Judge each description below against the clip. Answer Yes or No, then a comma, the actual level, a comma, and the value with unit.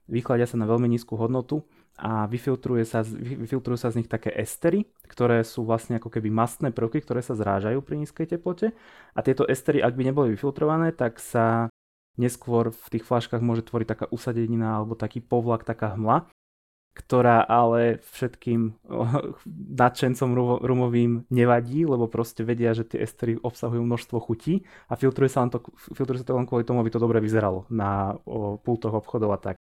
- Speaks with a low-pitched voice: Yes, low, 120 Hz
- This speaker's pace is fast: Yes, fast, 170 wpm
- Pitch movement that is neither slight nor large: No, narrow, 1.9 semitones